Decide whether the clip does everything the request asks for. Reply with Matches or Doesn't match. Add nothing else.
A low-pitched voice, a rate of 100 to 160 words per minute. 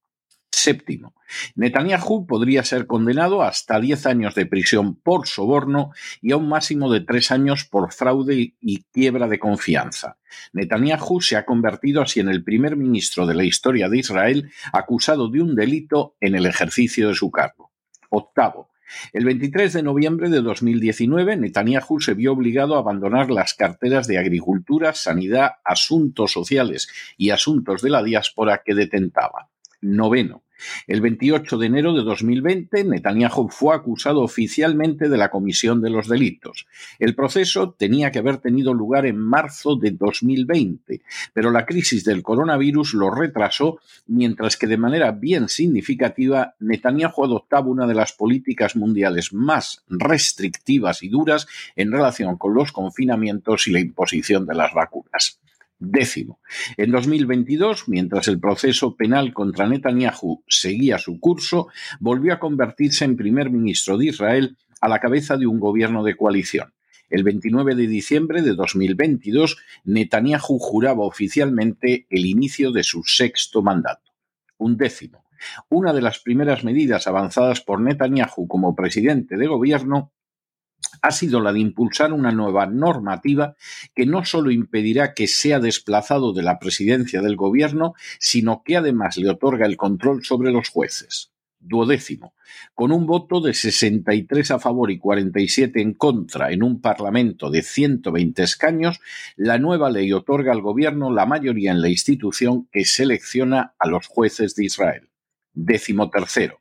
Matches